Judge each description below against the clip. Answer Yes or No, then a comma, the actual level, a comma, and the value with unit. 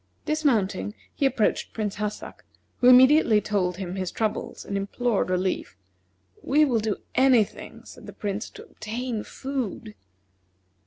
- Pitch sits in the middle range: No, high, 215 Hz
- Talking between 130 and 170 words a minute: Yes, average, 140 wpm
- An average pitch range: Yes, average, 4.3 semitones